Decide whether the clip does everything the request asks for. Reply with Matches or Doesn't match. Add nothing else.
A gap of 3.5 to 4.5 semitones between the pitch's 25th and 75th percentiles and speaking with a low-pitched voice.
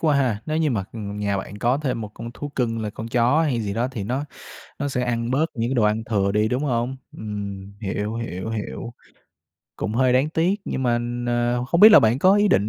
Matches